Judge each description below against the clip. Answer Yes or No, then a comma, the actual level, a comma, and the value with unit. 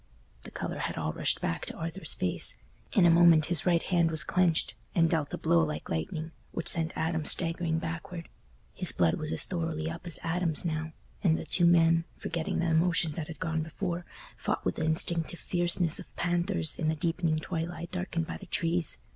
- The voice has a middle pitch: Yes, medium, 165 Hz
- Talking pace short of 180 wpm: No, average, 195 wpm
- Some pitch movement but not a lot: No, narrow, 1.5 semitones